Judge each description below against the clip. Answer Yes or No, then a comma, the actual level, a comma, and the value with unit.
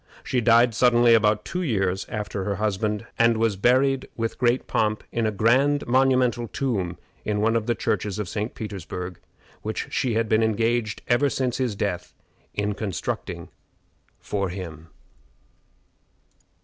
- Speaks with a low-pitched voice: Yes, low, 110 Hz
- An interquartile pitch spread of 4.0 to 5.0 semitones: No, average, 2.8 semitones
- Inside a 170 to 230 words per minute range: No, average, 150 wpm